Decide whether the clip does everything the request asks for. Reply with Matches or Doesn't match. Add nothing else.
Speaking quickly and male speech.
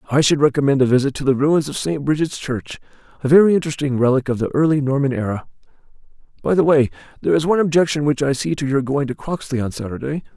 Matches